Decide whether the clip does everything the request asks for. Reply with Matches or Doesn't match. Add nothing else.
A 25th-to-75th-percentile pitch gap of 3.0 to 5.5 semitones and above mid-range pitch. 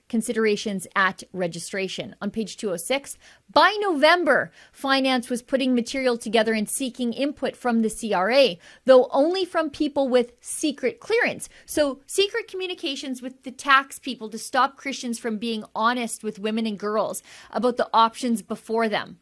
Matches